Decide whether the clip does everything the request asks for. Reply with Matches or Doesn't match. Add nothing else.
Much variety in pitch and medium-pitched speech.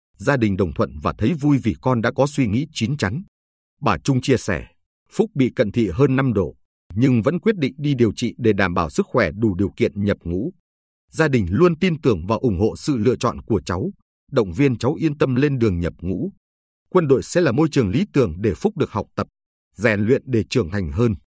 Doesn't match